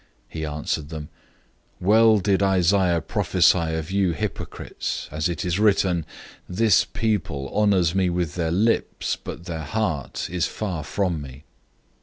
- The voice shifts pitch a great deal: No, average, 3.6 semitones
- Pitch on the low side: Yes, very low, 90 Hz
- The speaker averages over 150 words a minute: No, average, 145 wpm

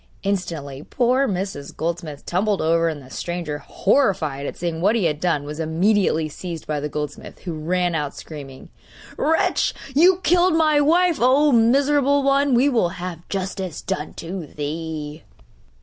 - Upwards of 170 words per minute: No, average, 160 wpm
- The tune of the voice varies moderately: No, wide, 8.5 semitones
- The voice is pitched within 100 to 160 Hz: No, medium, 175 Hz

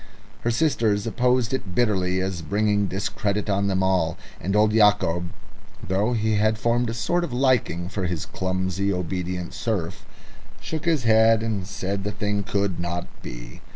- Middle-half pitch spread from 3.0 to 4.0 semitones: Yes, average, 3.3 semitones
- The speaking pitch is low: Yes, low, 100 Hz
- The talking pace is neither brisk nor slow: Yes, average, 160 wpm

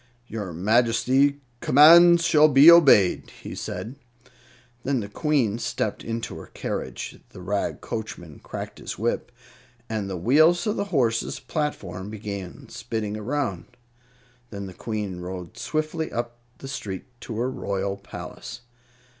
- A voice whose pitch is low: Yes, low, 115 Hz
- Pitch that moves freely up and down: Yes, wide, 6.3 semitones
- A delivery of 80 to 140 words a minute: Yes, slow, 135 wpm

